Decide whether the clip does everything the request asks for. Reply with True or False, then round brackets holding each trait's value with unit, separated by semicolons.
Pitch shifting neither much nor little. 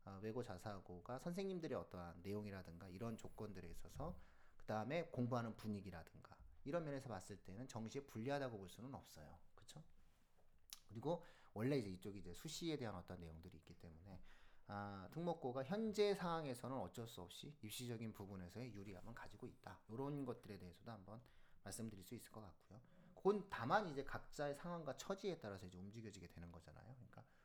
False (6.4 semitones)